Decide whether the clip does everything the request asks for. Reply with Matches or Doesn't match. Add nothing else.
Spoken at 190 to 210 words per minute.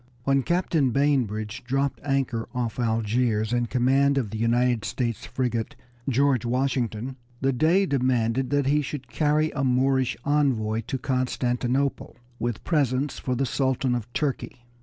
Doesn't match